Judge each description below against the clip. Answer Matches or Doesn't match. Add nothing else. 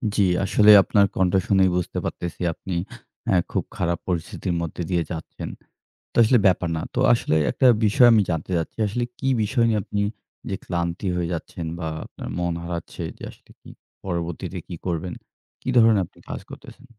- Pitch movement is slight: Doesn't match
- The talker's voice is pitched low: Matches